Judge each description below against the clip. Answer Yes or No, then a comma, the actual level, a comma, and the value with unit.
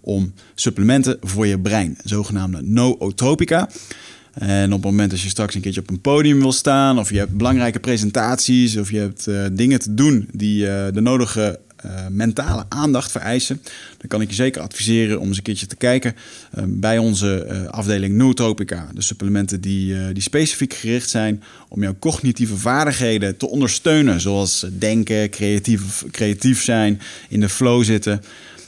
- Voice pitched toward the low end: Yes, low, 105 Hz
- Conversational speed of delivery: Yes, average, 170 wpm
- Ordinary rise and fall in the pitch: Yes, average, 3.8 semitones